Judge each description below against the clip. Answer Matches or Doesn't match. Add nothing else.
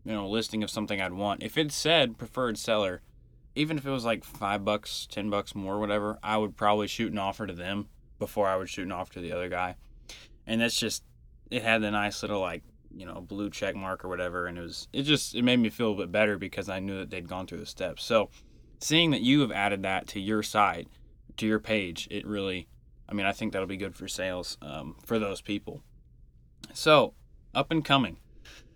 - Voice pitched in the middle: Doesn't match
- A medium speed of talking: Doesn't match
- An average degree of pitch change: Matches